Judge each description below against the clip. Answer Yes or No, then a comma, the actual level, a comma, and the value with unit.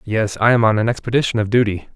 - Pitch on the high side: No, low, 110 Hz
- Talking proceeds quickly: Yes, fast, 245 wpm